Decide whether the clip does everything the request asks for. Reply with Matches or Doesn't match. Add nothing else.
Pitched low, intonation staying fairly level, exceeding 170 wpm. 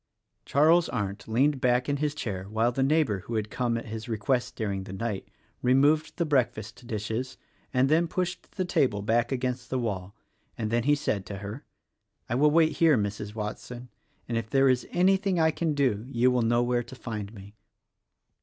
Doesn't match